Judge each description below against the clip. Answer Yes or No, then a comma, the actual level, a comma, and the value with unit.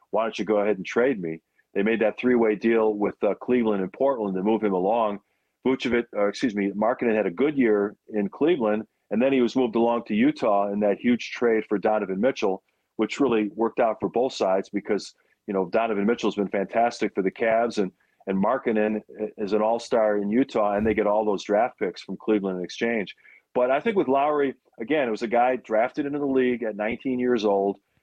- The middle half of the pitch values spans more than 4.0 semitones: No, average, 2.8 semitones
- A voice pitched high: No, low, 110 Hz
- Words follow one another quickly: Yes, fast, 225 wpm